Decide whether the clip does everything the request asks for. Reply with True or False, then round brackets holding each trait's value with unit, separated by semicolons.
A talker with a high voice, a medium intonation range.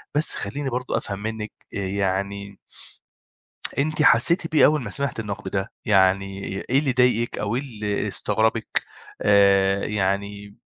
False (105 Hz; 4.1 semitones)